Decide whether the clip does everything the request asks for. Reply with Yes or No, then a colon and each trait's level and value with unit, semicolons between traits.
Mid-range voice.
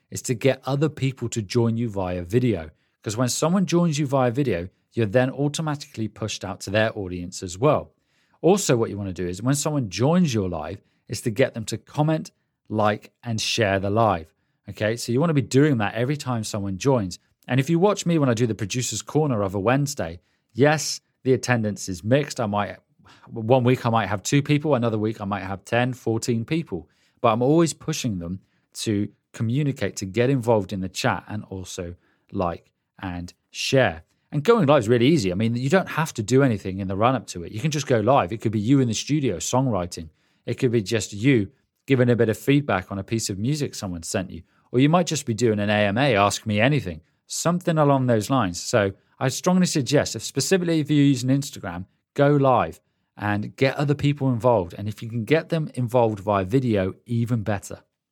No: low, 120 Hz